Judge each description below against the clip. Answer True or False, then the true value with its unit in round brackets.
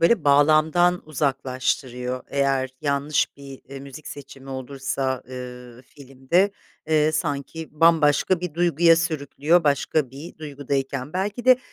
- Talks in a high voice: False (145 Hz)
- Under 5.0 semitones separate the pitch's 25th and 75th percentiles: True (3.3 semitones)